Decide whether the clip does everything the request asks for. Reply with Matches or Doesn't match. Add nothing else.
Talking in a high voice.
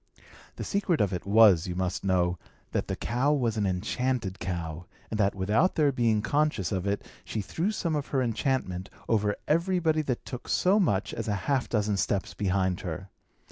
Doesn't match